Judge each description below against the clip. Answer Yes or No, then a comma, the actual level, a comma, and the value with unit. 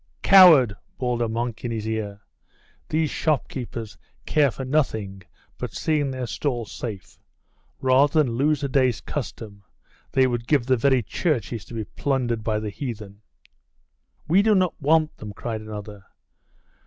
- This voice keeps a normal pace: Yes, average, 150 wpm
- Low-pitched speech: Yes, low, 120 Hz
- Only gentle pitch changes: No, average, 4.7 semitones